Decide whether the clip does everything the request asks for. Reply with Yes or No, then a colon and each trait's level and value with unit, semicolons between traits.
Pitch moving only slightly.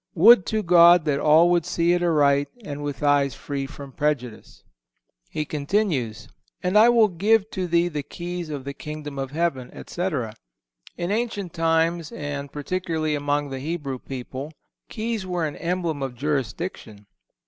No: average, 3.8 semitones